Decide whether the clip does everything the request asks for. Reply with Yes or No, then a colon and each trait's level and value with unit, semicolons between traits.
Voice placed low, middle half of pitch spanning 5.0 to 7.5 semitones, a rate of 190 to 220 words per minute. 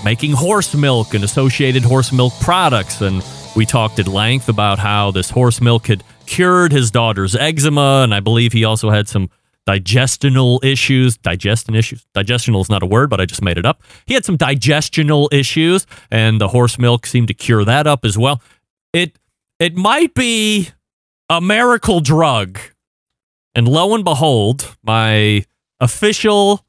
No: low, 125 Hz; wide, 5.4 semitones; average, 165 wpm